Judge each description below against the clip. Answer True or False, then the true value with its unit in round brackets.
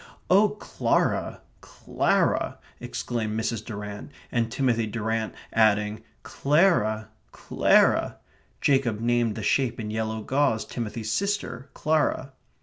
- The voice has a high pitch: False (115 Hz)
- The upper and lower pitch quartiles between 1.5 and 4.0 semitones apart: True (3.6 semitones)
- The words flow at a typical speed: False (105 wpm)